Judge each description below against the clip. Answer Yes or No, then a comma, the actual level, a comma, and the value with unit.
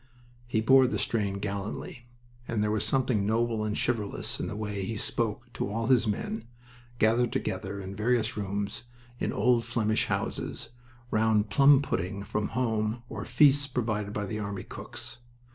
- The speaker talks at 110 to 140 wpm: No, average, 160 wpm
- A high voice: No, low, 110 Hz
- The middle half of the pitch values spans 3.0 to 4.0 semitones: No, narrow, 2.5 semitones